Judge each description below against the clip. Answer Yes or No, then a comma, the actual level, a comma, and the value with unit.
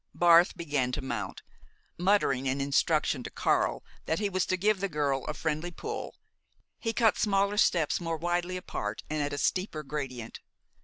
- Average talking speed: Yes, average, 170 wpm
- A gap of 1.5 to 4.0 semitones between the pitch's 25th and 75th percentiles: No, average, 4.8 semitones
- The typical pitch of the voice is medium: Yes, medium, 160 Hz